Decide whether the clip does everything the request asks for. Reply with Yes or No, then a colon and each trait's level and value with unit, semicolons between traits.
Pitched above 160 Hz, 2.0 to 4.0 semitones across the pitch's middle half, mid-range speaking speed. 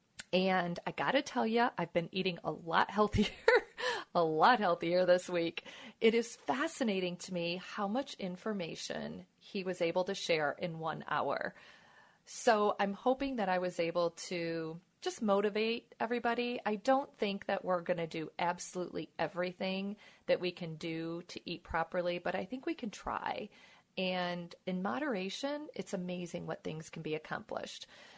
No: medium, 185 Hz; average, 4.5 semitones; average, 160 wpm